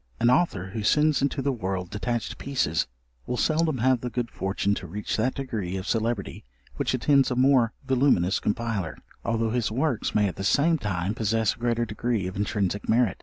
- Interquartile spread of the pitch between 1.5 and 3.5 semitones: No, average, 4.1 semitones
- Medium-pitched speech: No, low, 115 Hz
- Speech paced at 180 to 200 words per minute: Yes, average, 190 wpm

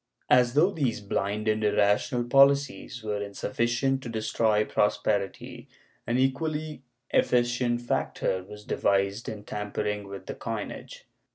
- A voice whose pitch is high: No, low, 110 Hz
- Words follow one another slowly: Yes, slow, 120 wpm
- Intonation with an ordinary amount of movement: Yes, average, 3.6 semitones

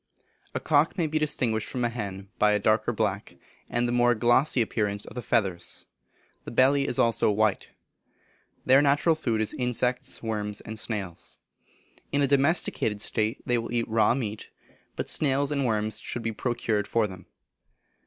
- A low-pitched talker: Yes, low, 115 Hz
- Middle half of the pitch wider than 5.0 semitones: No, average, 3.6 semitones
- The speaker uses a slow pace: No, average, 170 wpm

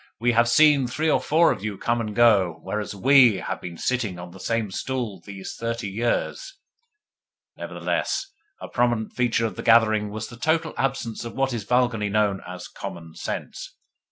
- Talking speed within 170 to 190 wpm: Yes, average, 180 wpm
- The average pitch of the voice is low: Yes, low, 115 Hz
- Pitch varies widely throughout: No, average, 3.4 semitones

